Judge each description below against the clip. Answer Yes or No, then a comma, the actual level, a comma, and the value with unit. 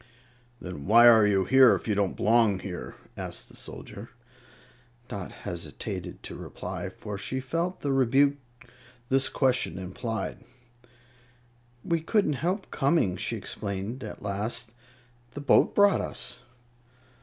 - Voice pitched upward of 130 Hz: No, low, 115 Hz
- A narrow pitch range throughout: No, wide, 5.5 semitones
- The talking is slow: Yes, slow, 130 wpm